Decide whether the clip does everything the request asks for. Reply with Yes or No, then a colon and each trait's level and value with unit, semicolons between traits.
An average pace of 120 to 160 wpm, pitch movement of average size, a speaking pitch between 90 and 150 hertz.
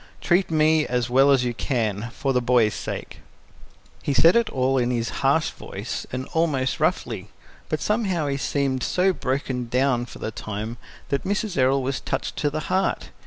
No: average, 180 wpm; average, 4.2 semitones; low, 135 Hz